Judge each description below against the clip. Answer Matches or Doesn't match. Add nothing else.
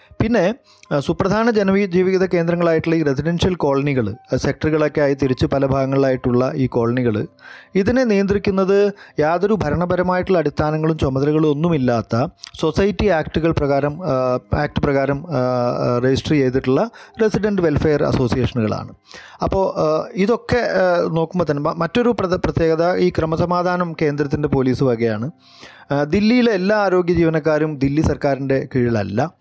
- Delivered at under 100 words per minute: Doesn't match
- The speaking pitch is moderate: Matches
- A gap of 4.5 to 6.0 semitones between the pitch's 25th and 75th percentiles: Matches